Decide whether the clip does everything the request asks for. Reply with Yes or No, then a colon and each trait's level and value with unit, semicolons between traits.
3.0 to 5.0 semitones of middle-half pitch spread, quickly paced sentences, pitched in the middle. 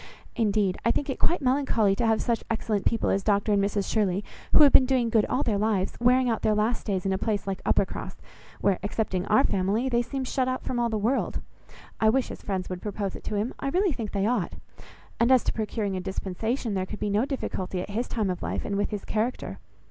No: average, 3.5 semitones; fast, 240 wpm; high, 215 Hz